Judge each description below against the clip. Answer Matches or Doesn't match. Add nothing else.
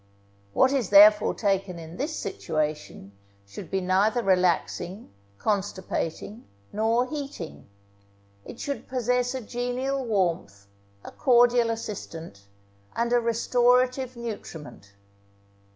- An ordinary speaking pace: Doesn't match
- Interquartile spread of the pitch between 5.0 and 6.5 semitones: Matches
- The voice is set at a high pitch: Matches